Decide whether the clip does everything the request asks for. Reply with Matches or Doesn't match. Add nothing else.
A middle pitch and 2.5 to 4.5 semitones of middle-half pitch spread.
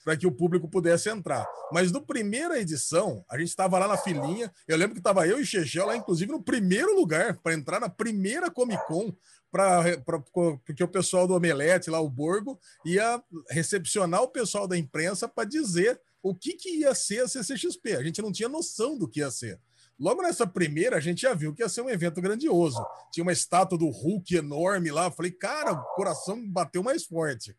Doesn't match